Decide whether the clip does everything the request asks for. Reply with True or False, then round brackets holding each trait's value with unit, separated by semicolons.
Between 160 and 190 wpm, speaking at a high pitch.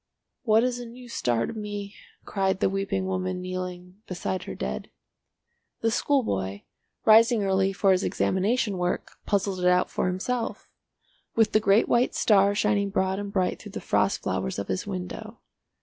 True (165 wpm; 195 Hz)